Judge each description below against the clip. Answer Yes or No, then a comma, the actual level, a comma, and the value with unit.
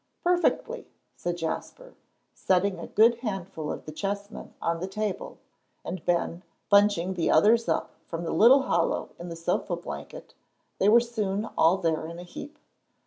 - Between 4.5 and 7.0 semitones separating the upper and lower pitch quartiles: Yes, average, 5.2 semitones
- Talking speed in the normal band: Yes, average, 160 wpm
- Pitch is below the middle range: No, high, 195 Hz